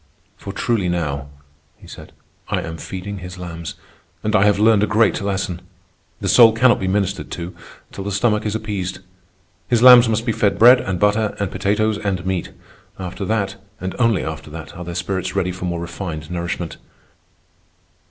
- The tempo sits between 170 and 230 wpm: Yes, average, 180 wpm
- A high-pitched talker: No, very low, 95 Hz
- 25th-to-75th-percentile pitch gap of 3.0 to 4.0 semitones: Yes, average, 3.3 semitones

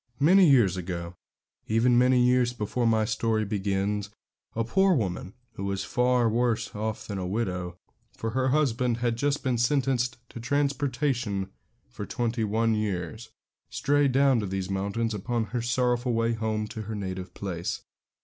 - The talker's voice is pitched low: Yes, low, 115 Hz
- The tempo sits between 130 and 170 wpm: Yes, average, 160 wpm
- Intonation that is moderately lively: Yes, average, 3.6 semitones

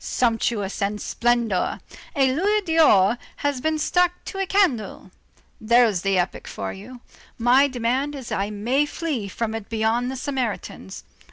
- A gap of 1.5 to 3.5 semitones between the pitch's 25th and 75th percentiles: No, average, 5.1 semitones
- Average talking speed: Yes, average, 155 wpm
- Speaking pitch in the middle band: No, high, 240 Hz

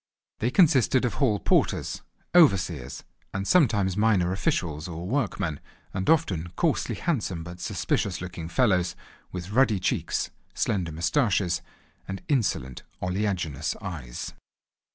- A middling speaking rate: No, slow, 115 wpm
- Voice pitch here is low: Yes, very low, 95 Hz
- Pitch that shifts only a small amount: No, average, 4.6 semitones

